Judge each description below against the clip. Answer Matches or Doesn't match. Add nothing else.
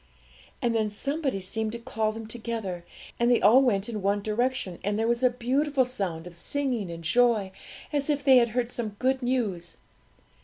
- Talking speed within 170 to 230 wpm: Matches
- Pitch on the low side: Doesn't match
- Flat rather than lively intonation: Doesn't match